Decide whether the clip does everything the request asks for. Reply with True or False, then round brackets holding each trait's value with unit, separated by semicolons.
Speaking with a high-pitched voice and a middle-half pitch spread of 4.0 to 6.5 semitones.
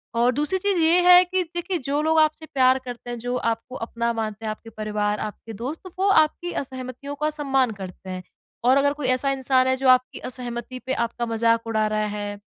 True (255 Hz; 4.5 semitones)